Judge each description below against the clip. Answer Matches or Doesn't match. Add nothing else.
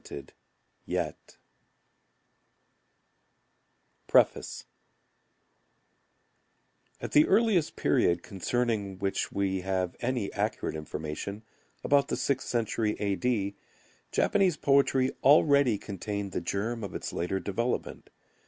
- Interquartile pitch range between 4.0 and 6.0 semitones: Matches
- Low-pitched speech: Matches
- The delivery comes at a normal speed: Doesn't match